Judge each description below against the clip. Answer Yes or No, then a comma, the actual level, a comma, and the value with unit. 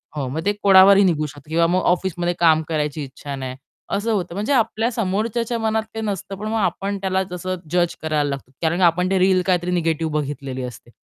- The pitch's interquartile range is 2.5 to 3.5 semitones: No, average, 4.6 semitones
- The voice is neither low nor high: Yes, medium, 180 Hz